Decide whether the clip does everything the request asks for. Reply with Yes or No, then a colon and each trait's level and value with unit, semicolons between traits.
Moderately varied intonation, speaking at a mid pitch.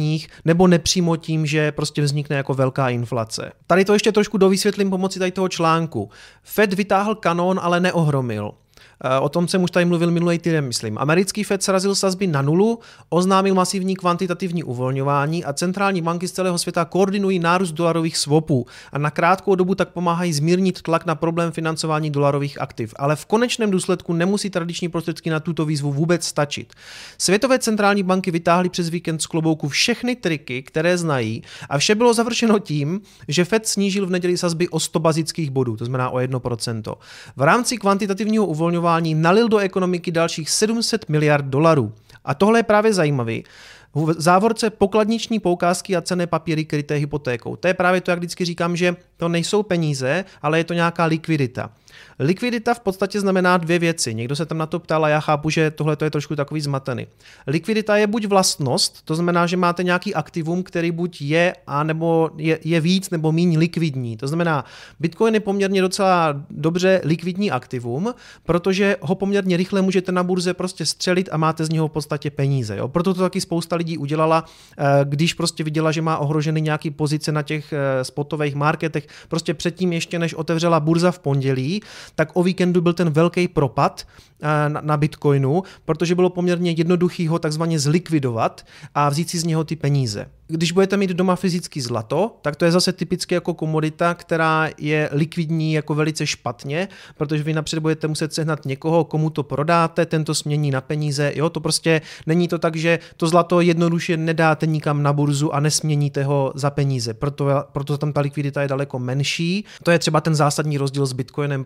Yes: average, 3.3 semitones; medium, 165 Hz